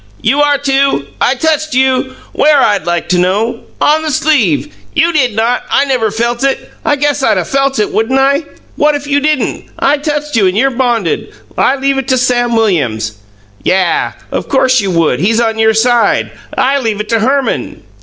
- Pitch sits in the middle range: No, very high, 255 Hz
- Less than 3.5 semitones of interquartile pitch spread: No, average, 4.2 semitones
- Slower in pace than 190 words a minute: No, average, 195 wpm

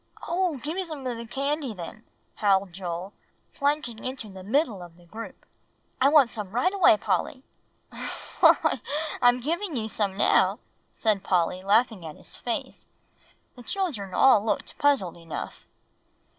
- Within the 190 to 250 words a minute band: No, average, 150 wpm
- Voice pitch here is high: Yes, high, 230 Hz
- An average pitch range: No, wide, 6.5 semitones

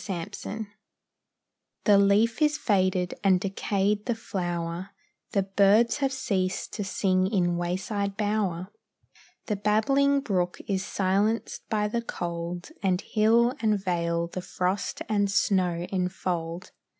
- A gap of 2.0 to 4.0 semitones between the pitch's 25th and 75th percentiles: Yes, average, 2.8 semitones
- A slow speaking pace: Yes, slow, 125 wpm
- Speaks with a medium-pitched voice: No, high, 195 Hz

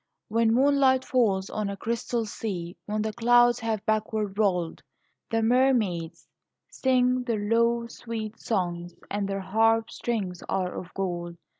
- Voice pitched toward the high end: Yes, high, 220 Hz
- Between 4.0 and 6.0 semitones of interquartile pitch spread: No, average, 3.5 semitones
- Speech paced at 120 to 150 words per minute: Yes, average, 140 wpm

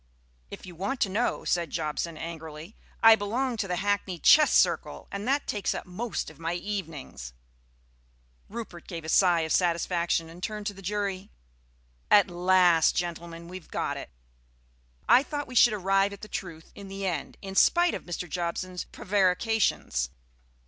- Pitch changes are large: No, average, 3.4 semitones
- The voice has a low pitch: No, medium, 185 Hz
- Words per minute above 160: Yes, average, 170 wpm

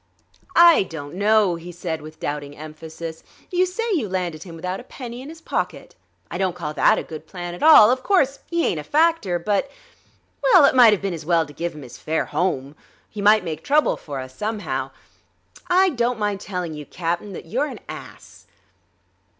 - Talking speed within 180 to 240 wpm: Yes, average, 200 wpm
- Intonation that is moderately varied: No, wide, 7.6 semitones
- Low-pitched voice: No, medium, 185 Hz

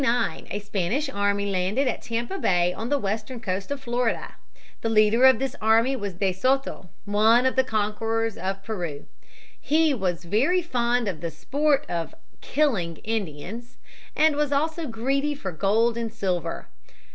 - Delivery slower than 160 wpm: No, average, 165 wpm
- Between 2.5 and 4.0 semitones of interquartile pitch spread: No, average, 5.2 semitones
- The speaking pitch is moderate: No, high, 225 Hz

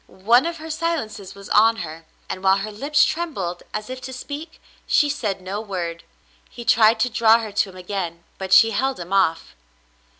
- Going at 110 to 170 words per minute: No, average, 195 wpm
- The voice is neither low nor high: No, high, 215 Hz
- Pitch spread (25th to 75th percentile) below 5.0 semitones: No, average, 5.3 semitones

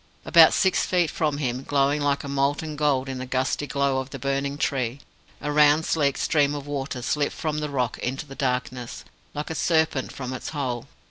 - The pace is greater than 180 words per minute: Yes, average, 195 wpm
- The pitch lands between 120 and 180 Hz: Yes, medium, 140 Hz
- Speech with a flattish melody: Yes, narrow, 2.2 semitones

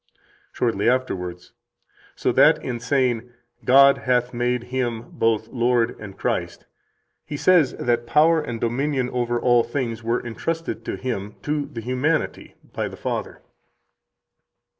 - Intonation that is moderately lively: No, narrow, 2.3 semitones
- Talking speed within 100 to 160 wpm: Yes, slow, 135 wpm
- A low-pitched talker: Yes, low, 125 Hz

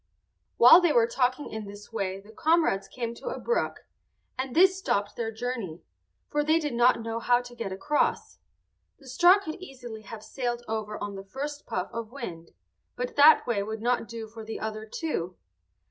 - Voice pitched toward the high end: Yes, high, 235 Hz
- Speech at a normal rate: Yes, average, 190 wpm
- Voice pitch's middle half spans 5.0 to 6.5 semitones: No, average, 4.3 semitones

